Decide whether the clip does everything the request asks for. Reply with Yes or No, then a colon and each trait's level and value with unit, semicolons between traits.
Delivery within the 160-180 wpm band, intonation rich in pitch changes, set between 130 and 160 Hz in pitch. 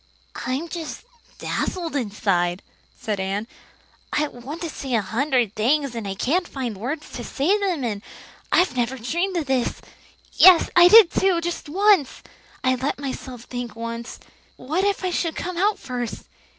No: average, 165 wpm; wide, 6.5 semitones; very high, 270 Hz